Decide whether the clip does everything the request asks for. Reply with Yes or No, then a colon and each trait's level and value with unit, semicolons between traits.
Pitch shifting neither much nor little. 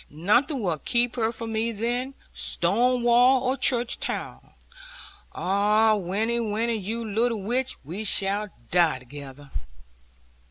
Yes: average, 3.5 semitones